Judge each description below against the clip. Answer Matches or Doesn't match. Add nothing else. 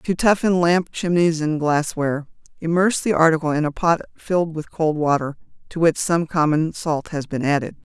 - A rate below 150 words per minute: Doesn't match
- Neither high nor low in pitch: Matches